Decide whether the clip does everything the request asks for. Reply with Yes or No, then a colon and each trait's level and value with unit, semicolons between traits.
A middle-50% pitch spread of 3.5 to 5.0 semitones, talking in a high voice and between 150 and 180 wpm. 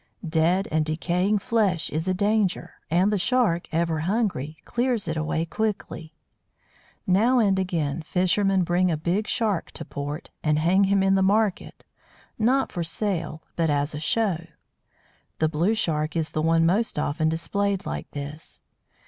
No: average, 4.2 semitones; medium, 175 Hz; average, 155 wpm